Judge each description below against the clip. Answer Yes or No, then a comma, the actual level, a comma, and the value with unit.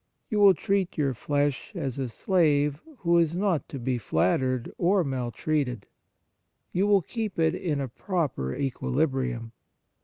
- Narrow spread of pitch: No, wide, 5.4 semitones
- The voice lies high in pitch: No, medium, 145 Hz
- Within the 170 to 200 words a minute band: No, average, 145 wpm